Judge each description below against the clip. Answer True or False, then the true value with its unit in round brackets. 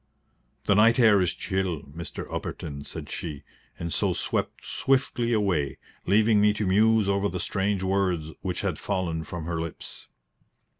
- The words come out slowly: False (155 wpm)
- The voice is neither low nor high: False (95 Hz)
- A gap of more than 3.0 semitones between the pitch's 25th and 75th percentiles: True (3.9 semitones)